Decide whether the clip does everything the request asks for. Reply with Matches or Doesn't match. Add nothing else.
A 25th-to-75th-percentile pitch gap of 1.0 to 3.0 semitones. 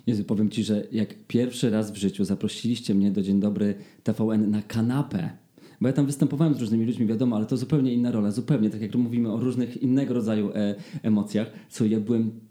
Matches